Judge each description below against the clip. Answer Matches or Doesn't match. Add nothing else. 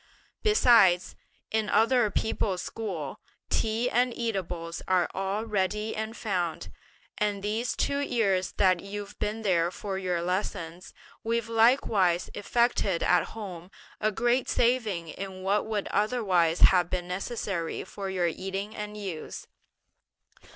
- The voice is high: Matches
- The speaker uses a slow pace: Matches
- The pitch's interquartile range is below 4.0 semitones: Matches